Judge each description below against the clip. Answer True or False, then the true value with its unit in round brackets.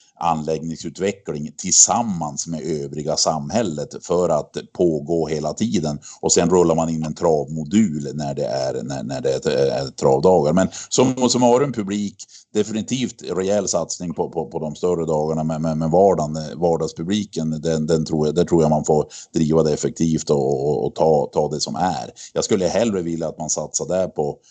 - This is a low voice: True (80 Hz)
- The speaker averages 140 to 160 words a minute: False (185 wpm)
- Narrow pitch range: False (4.5 semitones)